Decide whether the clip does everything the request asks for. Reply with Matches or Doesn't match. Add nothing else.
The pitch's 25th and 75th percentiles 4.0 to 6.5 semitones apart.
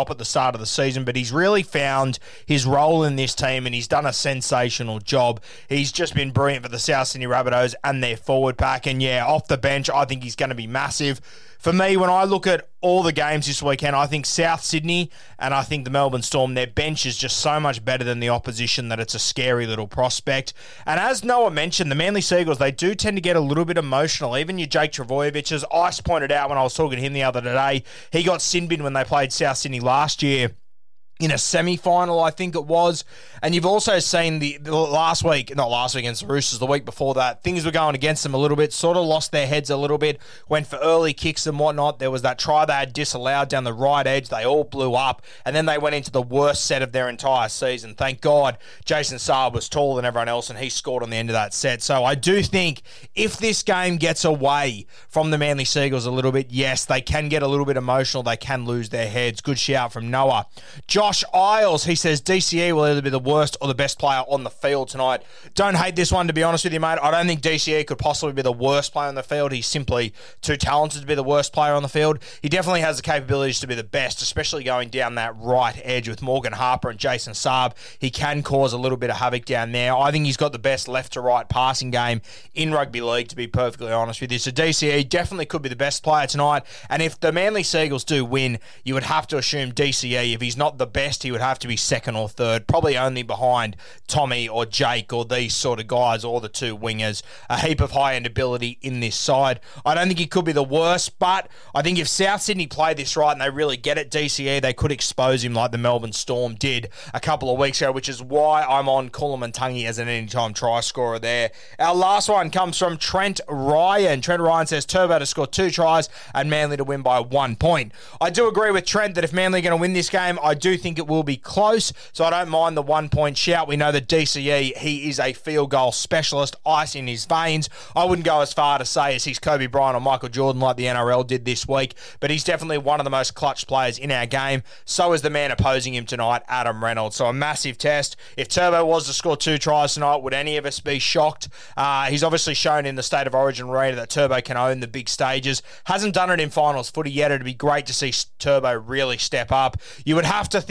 Doesn't match